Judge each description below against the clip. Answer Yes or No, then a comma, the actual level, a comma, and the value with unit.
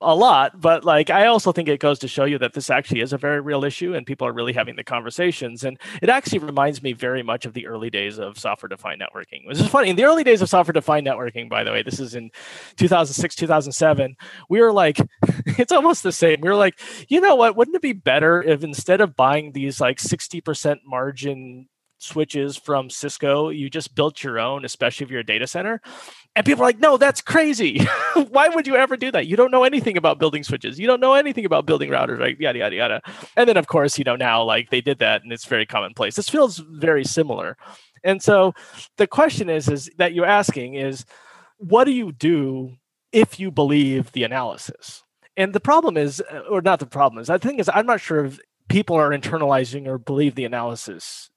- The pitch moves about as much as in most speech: No, wide, 7.0 semitones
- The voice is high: No, medium, 155 Hz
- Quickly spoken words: Yes, fast, 225 wpm